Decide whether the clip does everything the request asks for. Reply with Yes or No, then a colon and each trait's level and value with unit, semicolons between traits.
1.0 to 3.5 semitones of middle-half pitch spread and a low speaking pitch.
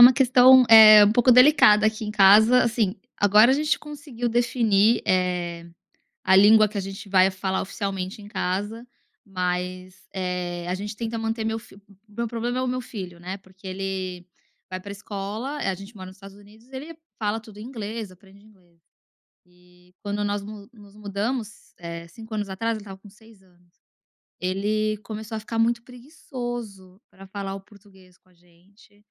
No: average, 3.1 semitones; high, 205 Hz